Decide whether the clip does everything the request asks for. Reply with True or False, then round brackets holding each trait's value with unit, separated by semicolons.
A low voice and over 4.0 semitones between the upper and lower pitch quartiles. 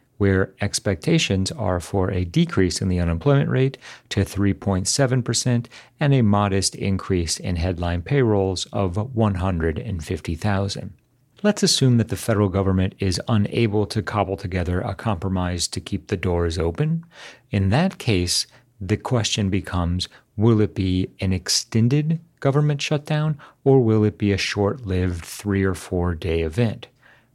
True (100 Hz; 4.7 semitones)